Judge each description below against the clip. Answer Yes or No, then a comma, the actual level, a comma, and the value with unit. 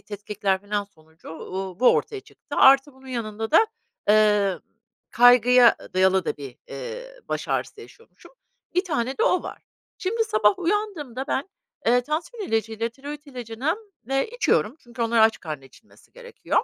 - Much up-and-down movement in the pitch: Yes, wide, 6.8 semitones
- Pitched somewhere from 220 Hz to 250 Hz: Yes, high, 240 Hz